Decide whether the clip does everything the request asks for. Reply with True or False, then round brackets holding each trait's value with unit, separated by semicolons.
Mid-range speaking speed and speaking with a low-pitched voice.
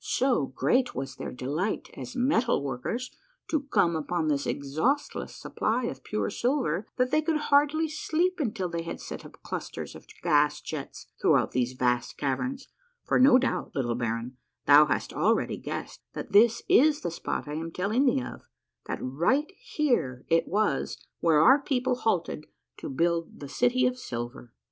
False (170 wpm; 175 Hz)